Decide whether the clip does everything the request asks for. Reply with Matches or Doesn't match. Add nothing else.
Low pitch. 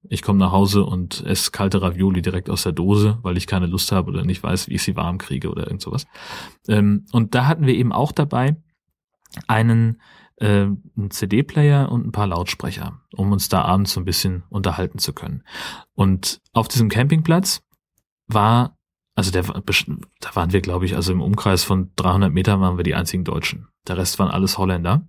Matches